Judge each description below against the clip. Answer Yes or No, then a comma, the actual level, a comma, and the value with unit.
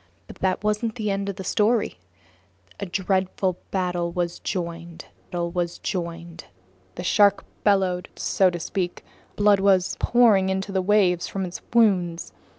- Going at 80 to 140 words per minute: Yes, slow, 135 wpm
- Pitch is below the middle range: No, medium, 185 Hz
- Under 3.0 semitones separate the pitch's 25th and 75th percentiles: Yes, narrow, 2.4 semitones